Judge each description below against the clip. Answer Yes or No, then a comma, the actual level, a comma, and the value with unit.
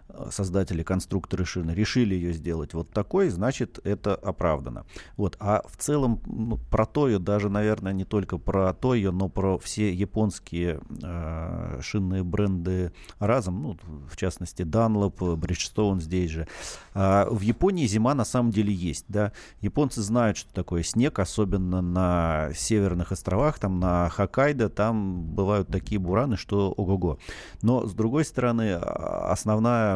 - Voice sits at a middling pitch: No, low, 100 Hz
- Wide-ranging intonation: No, average, 3.3 semitones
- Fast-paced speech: No, average, 145 wpm